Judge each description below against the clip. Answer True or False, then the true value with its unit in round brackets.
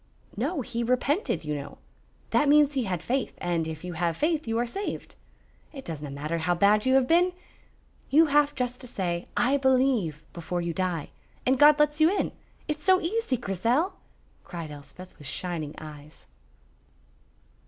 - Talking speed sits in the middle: True (170 wpm)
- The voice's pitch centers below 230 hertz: False (235 Hz)